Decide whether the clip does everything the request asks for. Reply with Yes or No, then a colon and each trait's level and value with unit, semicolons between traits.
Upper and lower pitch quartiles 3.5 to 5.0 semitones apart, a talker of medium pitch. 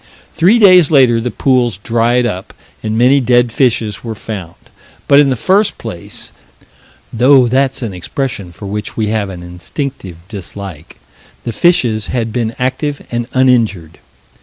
No: average, 4.1 semitones; low, 120 Hz